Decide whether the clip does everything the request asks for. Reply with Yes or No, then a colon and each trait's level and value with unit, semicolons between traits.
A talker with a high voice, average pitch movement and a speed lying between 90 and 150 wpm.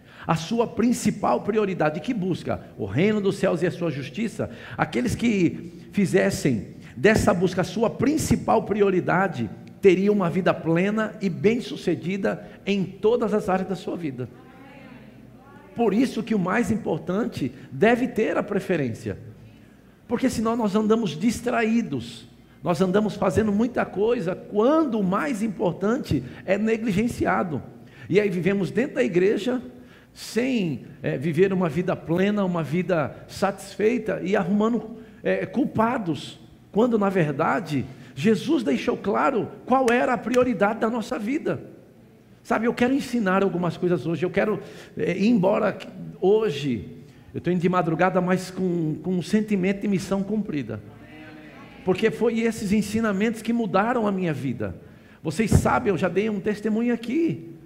Yes: high, 195 Hz; average, 4.9 semitones; average, 145 wpm